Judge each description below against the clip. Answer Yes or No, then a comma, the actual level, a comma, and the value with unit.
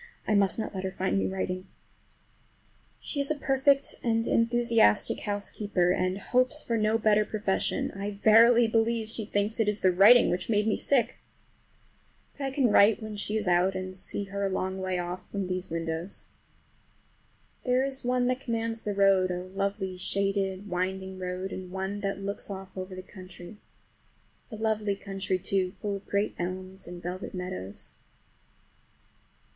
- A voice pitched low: No, high, 200 Hz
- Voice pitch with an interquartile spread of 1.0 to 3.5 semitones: Yes, average, 3.0 semitones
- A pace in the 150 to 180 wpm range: Yes, average, 170 wpm